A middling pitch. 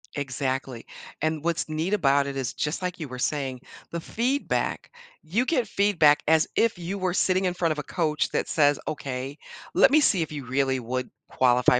Yes: medium, 155 Hz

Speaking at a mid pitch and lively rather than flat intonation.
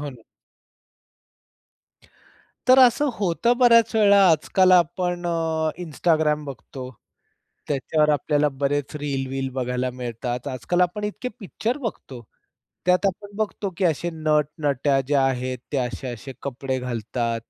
Yes: medium, 150 Hz; wide, 5.8 semitones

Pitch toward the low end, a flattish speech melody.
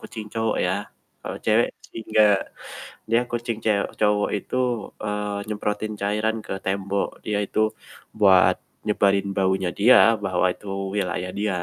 Yes: low, 105 Hz; narrow, 1.6 semitones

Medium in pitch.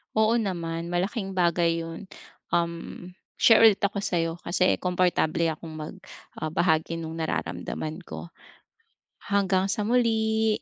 Yes: medium, 180 Hz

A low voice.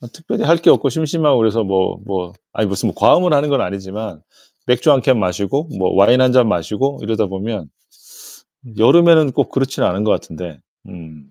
Yes: low, 110 Hz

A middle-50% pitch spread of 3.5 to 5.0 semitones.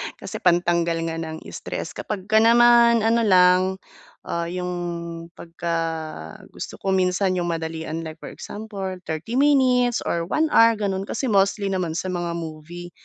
Yes: average, 4.5 semitones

